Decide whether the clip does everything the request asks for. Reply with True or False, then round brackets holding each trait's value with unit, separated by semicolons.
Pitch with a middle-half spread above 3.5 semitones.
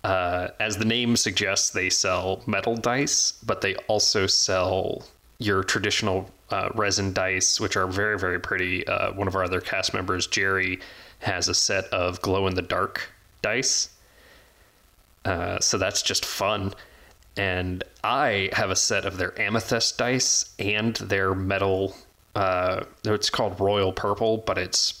False (2.5 semitones)